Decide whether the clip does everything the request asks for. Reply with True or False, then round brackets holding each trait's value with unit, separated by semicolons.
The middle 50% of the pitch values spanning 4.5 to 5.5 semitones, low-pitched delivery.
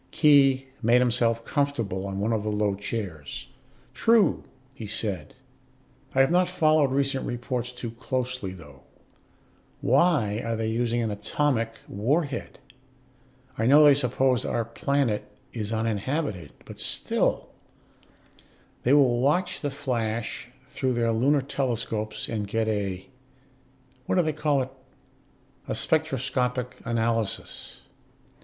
False (4.0 semitones; 120 Hz)